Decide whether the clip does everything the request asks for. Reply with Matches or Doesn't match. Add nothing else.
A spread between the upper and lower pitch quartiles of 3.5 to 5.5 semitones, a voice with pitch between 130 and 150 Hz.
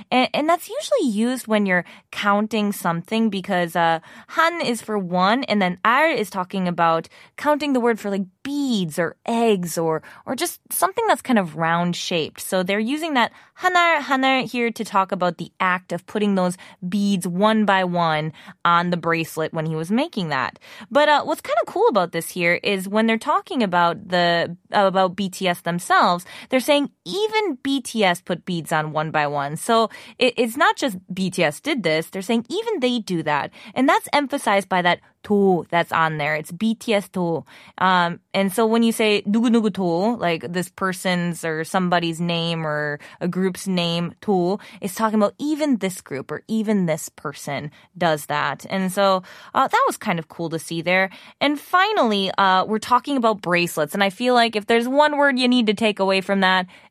Doesn't match